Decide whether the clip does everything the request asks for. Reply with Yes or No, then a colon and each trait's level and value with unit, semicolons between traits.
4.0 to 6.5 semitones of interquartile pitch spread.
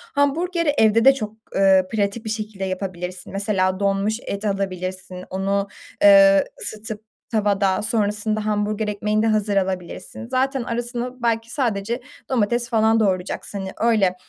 No: average, 2.7 semitones